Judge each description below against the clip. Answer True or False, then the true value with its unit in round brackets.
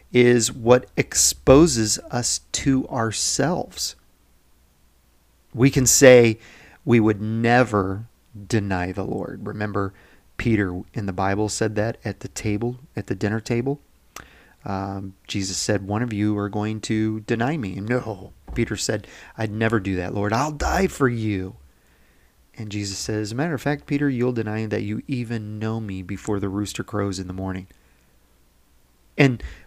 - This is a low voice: True (105 Hz)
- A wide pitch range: False (3.7 semitones)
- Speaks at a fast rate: False (155 wpm)